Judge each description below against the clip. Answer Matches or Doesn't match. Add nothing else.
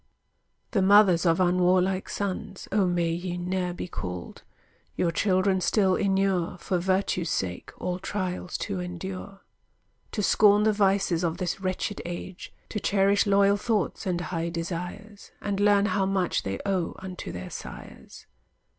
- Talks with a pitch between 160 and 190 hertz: Matches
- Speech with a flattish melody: Matches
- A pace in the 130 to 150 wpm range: Matches